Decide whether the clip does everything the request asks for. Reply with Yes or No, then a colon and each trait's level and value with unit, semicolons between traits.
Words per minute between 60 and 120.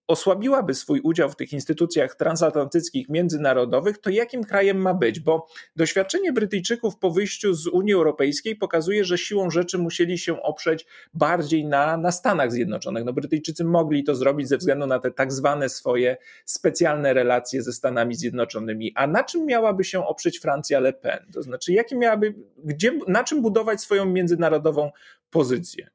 No: fast, 160 wpm